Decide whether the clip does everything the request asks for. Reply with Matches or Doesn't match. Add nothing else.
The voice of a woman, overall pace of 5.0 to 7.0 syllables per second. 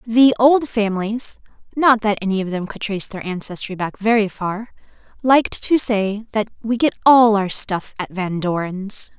Doesn't match